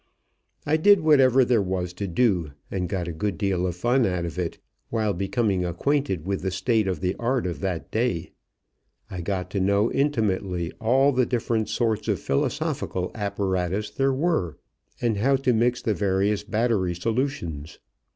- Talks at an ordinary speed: Yes, average, 170 wpm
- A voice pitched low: Yes, low, 100 Hz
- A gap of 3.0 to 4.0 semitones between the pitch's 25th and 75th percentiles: No, average, 5.0 semitones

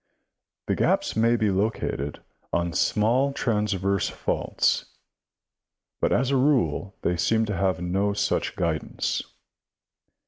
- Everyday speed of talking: No, slow, 115 wpm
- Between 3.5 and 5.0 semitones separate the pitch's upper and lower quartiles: Yes, average, 4.0 semitones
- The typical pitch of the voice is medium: No, low, 105 Hz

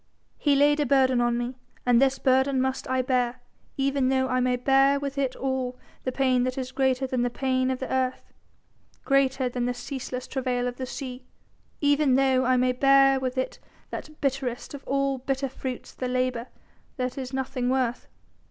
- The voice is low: No, very high, 260 Hz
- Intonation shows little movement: Yes, narrow, 1.3 semitones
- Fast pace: No, average, 190 wpm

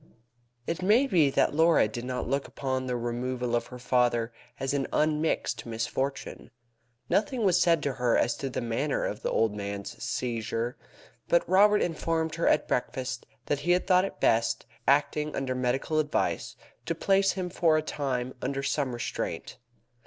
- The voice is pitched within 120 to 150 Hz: Yes, low, 135 Hz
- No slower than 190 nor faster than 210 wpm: No, average, 170 wpm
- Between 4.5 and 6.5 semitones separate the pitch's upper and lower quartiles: Yes, average, 4.9 semitones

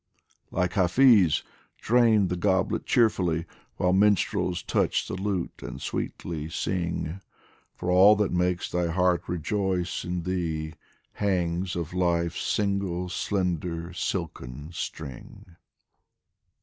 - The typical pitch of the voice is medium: No, very low, 90 Hz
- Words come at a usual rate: No, slow, 110 wpm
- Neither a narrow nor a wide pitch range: No, narrow, 2.1 semitones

